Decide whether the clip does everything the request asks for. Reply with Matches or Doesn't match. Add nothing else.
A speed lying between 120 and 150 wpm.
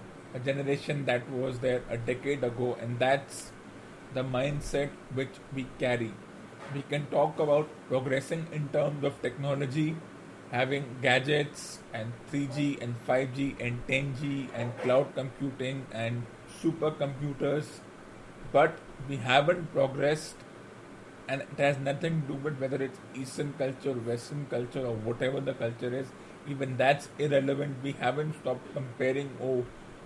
Matches